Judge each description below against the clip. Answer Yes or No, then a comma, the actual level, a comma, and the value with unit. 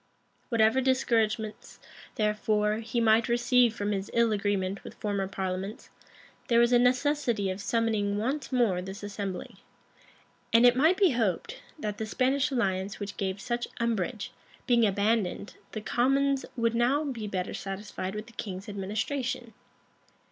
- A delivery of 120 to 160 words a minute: Yes, average, 150 wpm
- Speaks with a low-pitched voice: No, high, 220 Hz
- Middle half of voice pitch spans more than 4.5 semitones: No, average, 3.3 semitones